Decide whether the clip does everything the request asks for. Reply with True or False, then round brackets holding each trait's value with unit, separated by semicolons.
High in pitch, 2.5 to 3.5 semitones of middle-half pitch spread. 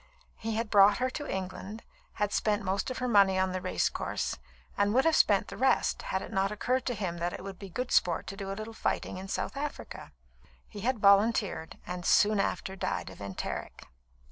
True (200 Hz; 3.1 semitones)